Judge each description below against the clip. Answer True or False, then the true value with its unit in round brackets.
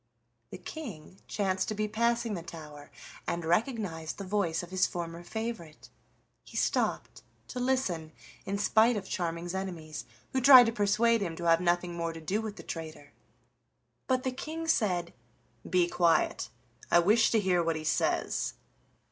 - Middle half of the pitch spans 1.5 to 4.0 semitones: False (5.0 semitones)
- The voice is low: False (185 Hz)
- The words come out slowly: False (165 wpm)